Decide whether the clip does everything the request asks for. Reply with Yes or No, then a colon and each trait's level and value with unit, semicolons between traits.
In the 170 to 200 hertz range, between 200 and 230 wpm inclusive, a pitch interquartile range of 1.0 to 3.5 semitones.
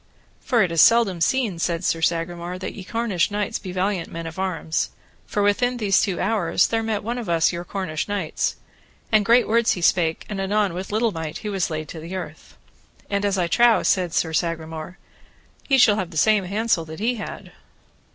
No: high, 190 Hz; fast, 205 wpm; average, 4.2 semitones